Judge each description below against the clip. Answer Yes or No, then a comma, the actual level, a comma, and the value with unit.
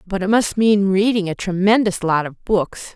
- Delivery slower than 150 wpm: No, fast, 205 wpm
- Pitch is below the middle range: No, high, 195 Hz